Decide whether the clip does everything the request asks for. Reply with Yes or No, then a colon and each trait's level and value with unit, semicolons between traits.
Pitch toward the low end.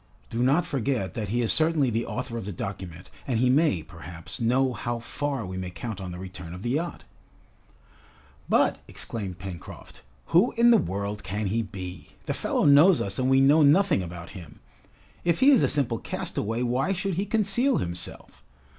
Yes: low, 115 Hz